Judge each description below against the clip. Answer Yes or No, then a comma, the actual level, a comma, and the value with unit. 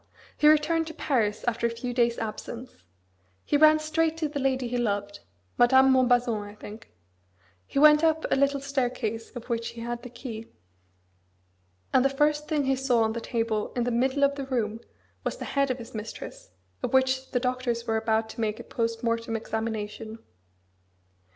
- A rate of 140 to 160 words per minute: No, average, 185 wpm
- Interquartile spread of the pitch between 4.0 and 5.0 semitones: No, average, 3.4 semitones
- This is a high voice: Yes, high, 245 Hz